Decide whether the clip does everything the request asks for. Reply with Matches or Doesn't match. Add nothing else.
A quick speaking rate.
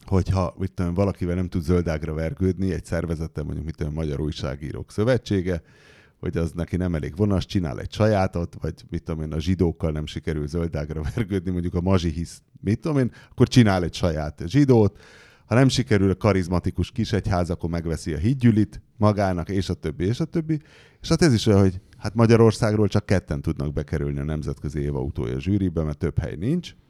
Doesn't match